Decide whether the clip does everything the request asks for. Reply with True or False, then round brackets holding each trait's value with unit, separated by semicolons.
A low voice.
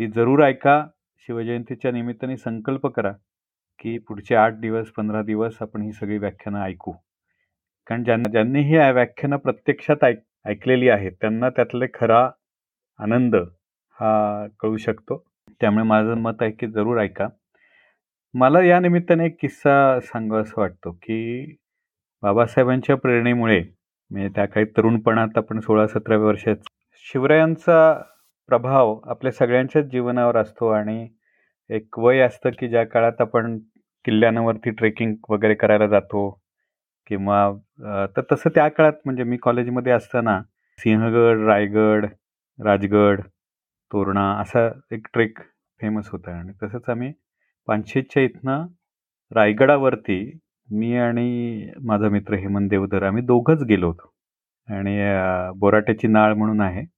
True (115 Hz)